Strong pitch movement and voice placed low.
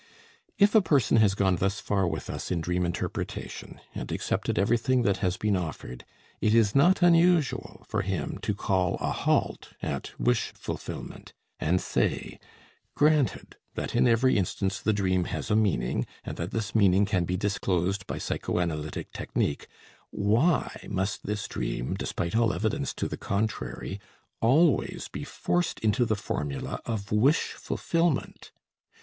No: average, 4.6 semitones; low, 100 Hz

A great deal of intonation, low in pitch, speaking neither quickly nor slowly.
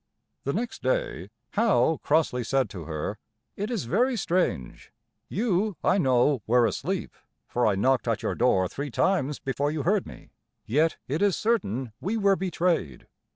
No: wide, 8.4 semitones; medium, 150 Hz; average, 160 wpm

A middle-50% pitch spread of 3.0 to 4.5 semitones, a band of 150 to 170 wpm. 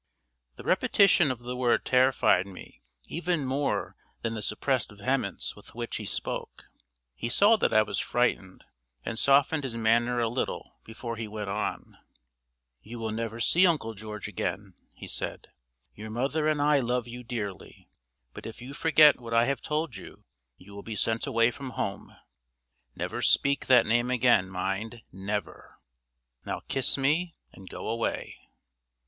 Yes: average, 3.8 semitones; average, 160 wpm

